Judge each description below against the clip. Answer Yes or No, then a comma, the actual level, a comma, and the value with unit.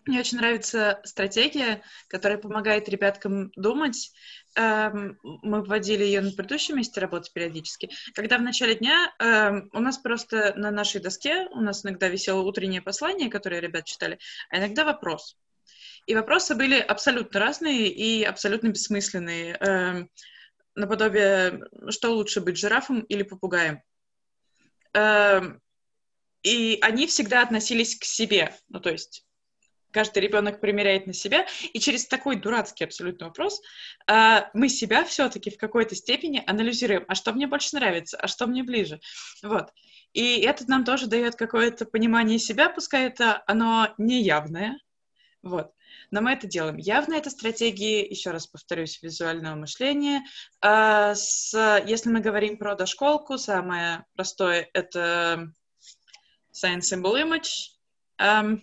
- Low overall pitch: No, high, 215 Hz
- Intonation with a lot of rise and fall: No, average, 3.6 semitones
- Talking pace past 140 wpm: No, average, 130 wpm